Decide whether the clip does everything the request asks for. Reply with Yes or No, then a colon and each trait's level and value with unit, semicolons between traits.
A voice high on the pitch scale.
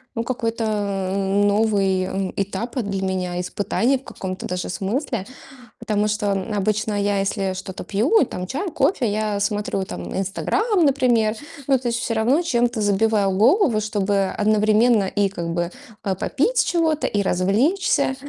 Yes: high, 210 Hz